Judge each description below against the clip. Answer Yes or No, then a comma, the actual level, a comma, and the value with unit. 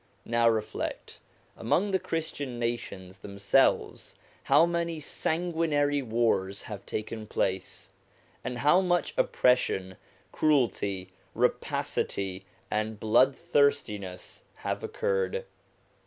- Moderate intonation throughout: No, wide, 7.8 semitones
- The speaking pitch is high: No, low, 120 Hz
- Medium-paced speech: No, slow, 90 wpm